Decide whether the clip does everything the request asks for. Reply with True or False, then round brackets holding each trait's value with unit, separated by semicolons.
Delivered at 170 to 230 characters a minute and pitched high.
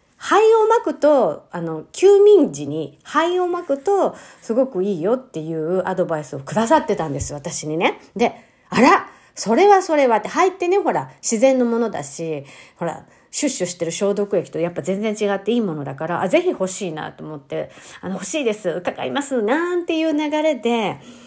False (360 characters per minute; 225 Hz)